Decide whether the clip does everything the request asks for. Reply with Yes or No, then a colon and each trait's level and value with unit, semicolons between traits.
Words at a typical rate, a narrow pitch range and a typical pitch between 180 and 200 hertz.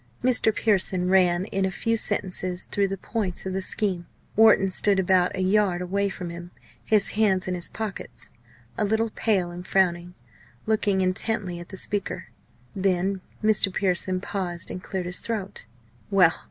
Yes: average, 165 wpm; narrow, 2.2 semitones; high, 190 Hz